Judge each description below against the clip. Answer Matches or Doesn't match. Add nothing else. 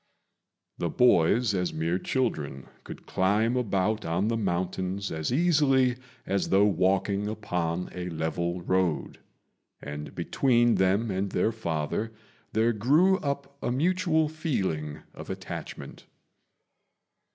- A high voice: Doesn't match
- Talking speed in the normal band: Doesn't match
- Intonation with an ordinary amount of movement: Doesn't match